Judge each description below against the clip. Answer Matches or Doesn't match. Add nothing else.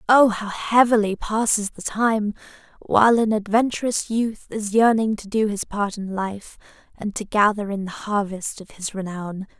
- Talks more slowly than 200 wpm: Matches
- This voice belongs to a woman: Matches